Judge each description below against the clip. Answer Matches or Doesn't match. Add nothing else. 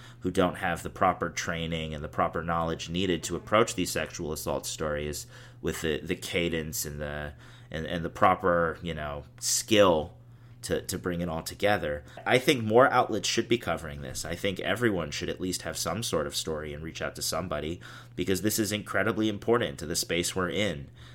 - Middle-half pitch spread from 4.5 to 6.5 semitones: Matches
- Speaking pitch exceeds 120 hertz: Doesn't match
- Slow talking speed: Doesn't match